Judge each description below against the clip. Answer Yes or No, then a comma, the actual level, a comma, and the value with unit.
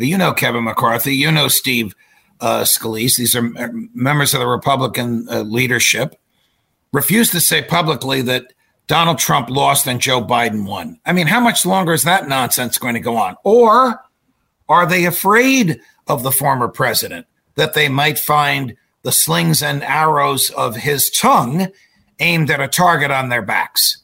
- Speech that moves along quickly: No, average, 165 wpm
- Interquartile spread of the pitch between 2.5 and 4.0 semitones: No, average, 5.2 semitones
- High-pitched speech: No, medium, 140 Hz